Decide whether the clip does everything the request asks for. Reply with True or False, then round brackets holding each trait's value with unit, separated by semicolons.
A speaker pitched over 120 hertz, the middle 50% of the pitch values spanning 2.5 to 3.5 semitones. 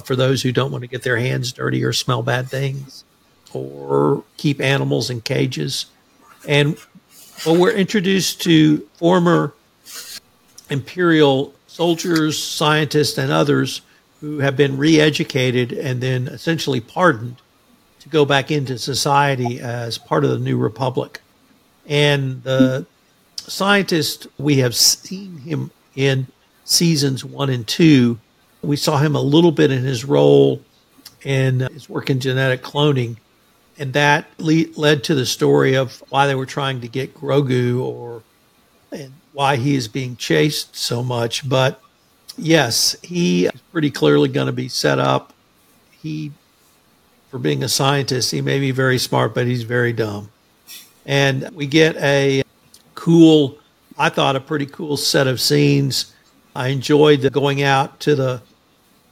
True (140 Hz; 3.0 semitones)